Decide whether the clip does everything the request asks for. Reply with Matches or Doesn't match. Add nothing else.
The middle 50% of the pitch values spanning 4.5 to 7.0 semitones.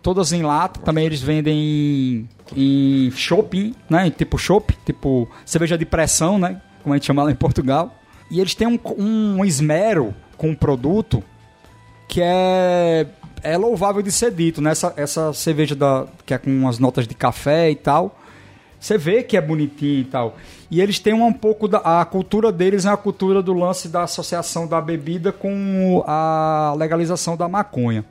Matches